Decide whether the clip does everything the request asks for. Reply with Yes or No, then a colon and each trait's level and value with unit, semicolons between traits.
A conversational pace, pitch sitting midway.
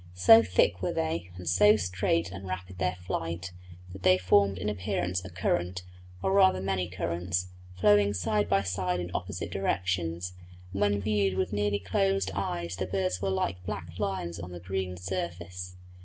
No: average, 170 wpm; very low, 90 Hz